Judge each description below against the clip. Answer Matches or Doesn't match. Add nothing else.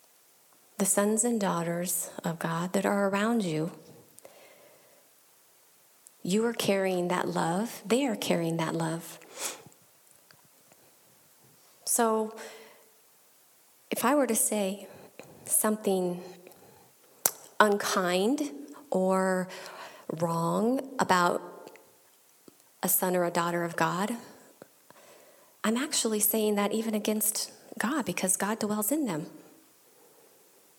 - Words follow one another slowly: Matches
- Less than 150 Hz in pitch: Doesn't match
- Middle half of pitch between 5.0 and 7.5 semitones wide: Doesn't match